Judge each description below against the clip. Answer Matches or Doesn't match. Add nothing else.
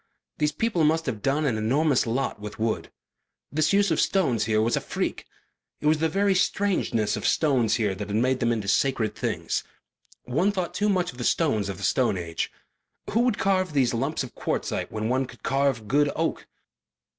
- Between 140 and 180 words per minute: Doesn't match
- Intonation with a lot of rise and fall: Matches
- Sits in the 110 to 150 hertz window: Matches